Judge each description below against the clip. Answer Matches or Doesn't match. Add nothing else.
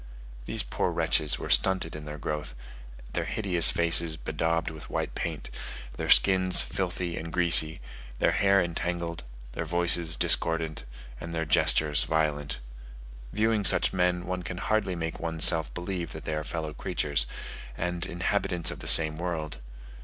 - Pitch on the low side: Matches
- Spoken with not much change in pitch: Matches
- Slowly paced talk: Doesn't match